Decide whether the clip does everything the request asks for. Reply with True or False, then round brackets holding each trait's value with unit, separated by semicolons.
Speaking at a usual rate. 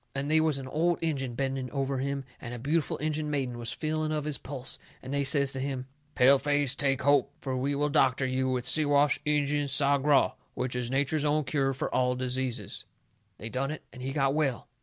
False (210 wpm)